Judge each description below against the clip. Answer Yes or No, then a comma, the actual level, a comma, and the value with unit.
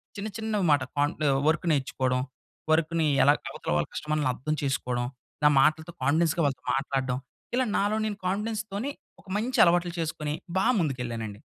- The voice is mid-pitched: Yes, medium, 155 Hz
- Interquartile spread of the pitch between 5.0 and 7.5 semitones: Yes, wide, 5.6 semitones